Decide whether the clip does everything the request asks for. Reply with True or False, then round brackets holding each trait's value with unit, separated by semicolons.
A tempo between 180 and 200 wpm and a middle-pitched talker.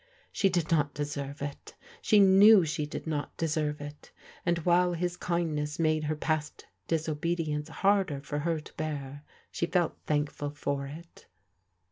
False (150 wpm; 155 Hz)